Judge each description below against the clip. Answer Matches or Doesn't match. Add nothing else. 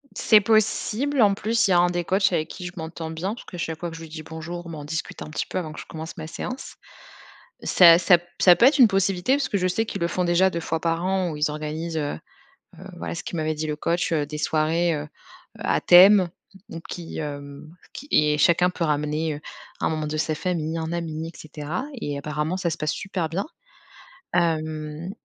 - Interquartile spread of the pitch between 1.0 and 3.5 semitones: Matches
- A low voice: Doesn't match